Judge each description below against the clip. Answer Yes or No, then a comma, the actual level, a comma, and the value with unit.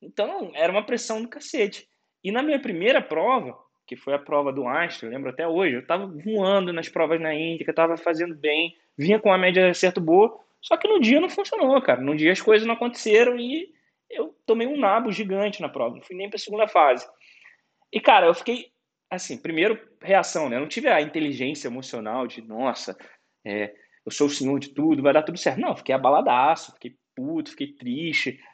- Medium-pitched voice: No, high, 195 Hz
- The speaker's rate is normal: No, fast, 210 wpm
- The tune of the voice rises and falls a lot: Yes, wide, 8.0 semitones